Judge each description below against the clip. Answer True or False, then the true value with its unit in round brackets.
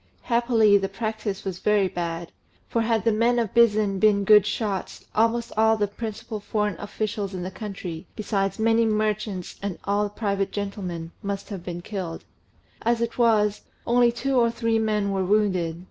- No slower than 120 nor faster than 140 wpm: False (165 wpm)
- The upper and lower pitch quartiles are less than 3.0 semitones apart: True (2.5 semitones)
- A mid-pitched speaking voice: False (210 Hz)